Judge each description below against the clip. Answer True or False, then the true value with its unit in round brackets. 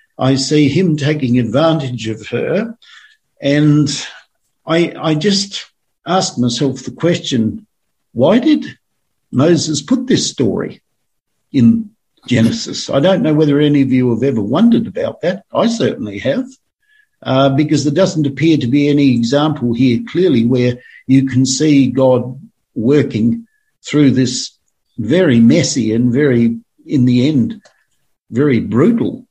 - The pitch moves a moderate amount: False (6.6 semitones)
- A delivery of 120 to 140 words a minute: True (135 wpm)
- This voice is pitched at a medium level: True (145 Hz)